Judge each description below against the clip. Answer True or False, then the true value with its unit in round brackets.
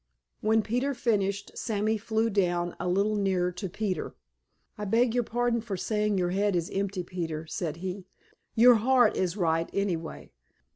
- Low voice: False (200 Hz)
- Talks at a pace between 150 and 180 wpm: True (160 wpm)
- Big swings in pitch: False (3.6 semitones)